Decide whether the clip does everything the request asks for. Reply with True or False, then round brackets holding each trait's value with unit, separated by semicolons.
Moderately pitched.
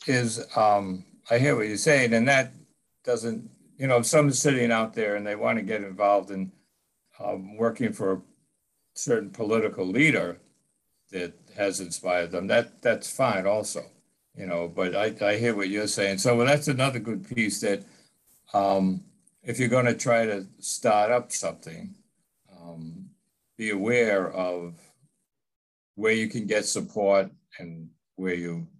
False (110 Hz)